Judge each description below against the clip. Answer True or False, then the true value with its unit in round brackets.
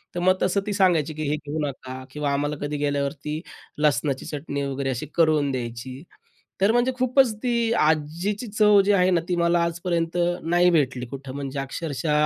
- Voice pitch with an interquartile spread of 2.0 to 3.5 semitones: False (4.4 semitones)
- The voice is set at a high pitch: False (155 Hz)